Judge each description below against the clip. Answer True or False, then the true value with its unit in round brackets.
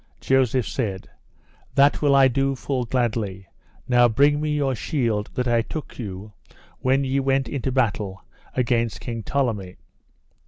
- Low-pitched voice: True (125 Hz)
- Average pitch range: True (3.6 semitones)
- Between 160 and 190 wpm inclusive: False (145 wpm)